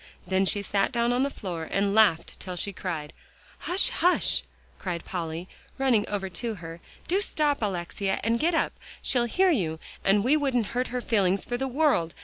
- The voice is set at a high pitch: Yes, high, 205 Hz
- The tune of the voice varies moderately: No, wide, 5.8 semitones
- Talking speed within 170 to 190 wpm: Yes, average, 185 wpm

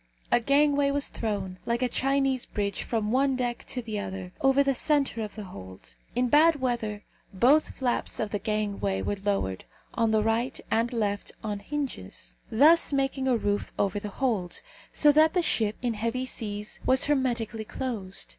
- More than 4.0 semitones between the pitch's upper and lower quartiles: Yes, average, 4.6 semitones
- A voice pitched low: No, high, 230 Hz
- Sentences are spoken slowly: No, average, 175 wpm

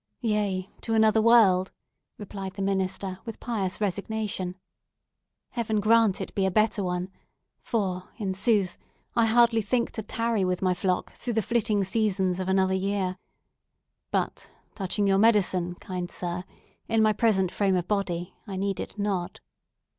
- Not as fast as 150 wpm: No, average, 155 wpm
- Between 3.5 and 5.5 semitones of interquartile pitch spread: No, average, 2.8 semitones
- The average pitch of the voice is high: Yes, high, 200 Hz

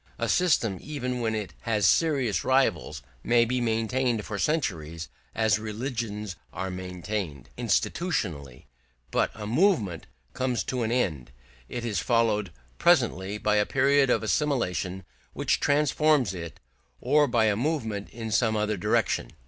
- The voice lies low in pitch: Yes, low, 110 Hz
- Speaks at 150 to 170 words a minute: No, average, 140 wpm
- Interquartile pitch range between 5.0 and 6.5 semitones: No, average, 4.4 semitones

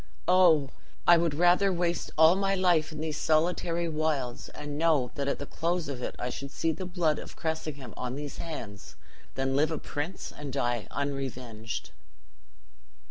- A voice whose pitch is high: No, medium, 155 Hz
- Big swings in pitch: No, average, 3.7 semitones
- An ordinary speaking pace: Yes, average, 170 wpm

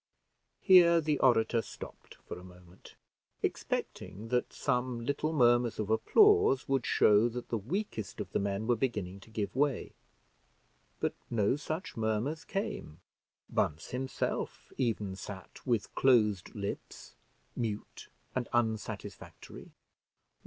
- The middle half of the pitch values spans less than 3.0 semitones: No, average, 4.7 semitones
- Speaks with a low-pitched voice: Yes, low, 120 Hz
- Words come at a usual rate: No, slow, 125 wpm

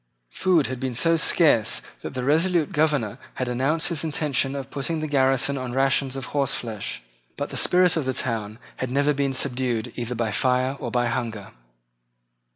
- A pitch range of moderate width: Yes, average, 3.2 semitones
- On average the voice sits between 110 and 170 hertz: Yes, low, 135 Hz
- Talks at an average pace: Yes, average, 180 wpm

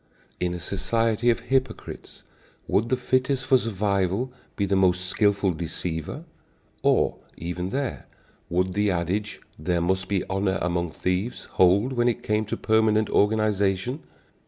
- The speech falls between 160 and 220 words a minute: No, average, 140 wpm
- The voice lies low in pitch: Yes, low, 100 Hz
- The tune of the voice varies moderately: Yes, average, 3.9 semitones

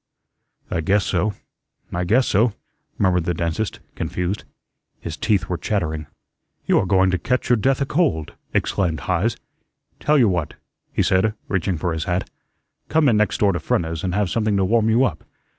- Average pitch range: Yes, average, 4.0 semitones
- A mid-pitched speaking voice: No, very low, 95 Hz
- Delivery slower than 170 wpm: No, average, 175 wpm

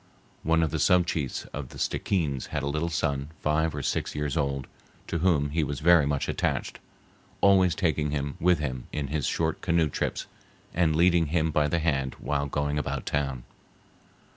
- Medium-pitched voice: No, very low, 75 Hz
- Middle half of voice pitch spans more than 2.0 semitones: Yes, narrow, 2.6 semitones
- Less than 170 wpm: No, average, 185 wpm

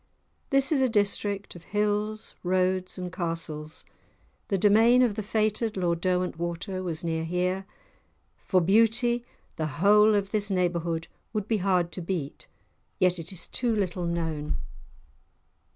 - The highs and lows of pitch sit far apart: No, average, 3.6 semitones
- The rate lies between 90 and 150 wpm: Yes, average, 140 wpm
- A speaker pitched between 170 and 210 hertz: Yes, medium, 185 Hz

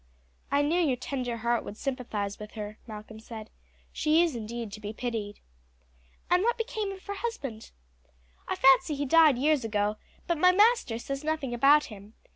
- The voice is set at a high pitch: Yes, very high, 255 Hz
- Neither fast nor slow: Yes, average, 175 wpm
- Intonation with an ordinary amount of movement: No, wide, 6.3 semitones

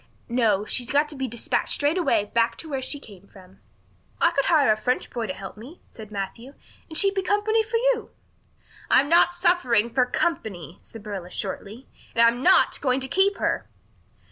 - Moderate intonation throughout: No, wide, 7.8 semitones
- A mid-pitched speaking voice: No, very high, 255 Hz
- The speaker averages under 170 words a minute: No, average, 195 wpm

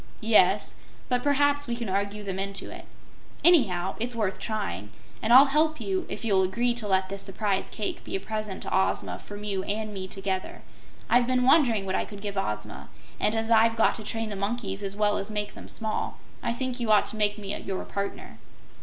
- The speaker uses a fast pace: Yes, fast, 210 wpm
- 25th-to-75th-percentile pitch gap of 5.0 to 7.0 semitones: No, average, 3.3 semitones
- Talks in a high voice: Yes, high, 210 Hz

